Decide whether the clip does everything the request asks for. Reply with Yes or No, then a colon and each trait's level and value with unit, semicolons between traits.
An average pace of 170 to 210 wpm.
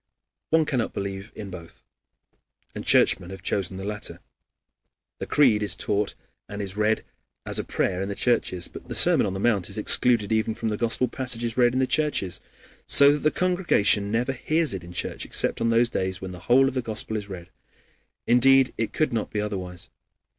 Yes: average, 200 wpm